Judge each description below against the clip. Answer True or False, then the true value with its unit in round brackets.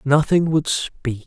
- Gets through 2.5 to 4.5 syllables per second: True (3.5 syllables/s)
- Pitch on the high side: False (145 Hz)